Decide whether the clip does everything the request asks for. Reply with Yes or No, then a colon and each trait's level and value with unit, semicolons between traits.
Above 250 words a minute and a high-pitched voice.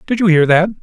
No: fast, 290 wpm; medium, 180 Hz